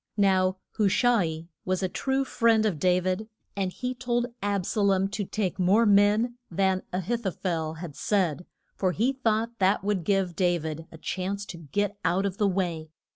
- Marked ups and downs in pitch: No, average, 3.0 semitones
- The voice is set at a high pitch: Yes, high, 195 Hz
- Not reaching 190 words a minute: No, average, 200 wpm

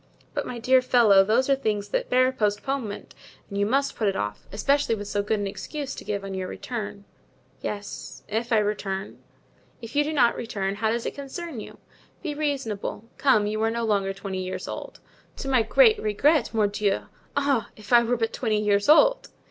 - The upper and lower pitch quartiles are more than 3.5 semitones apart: Yes, average, 4.3 semitones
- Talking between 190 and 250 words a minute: Yes, average, 195 wpm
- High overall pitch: Yes, high, 225 Hz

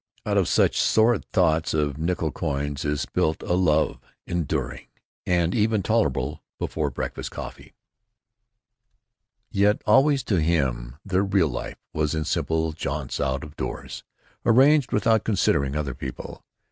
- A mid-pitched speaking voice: No, very low, 80 Hz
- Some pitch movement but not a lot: No, wide, 5.9 semitones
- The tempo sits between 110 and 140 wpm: Yes, slow, 135 wpm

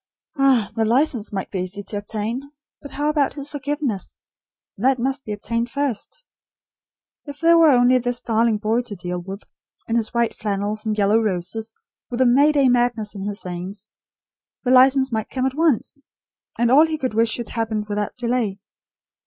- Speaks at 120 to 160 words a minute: No, average, 180 wpm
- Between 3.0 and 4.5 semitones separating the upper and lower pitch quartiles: Yes, average, 4.2 semitones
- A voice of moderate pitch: No, high, 235 Hz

